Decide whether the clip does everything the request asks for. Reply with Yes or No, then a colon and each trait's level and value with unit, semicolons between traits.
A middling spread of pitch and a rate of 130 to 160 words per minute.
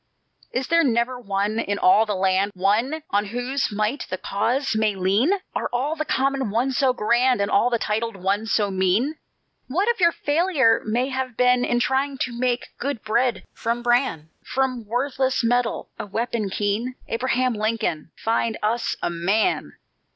No: average, 3.8 semitones; average, 170 wpm